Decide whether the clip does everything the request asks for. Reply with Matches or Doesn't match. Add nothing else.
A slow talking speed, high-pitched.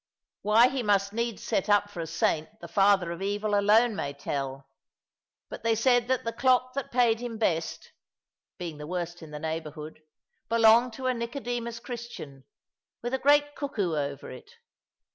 Doesn't match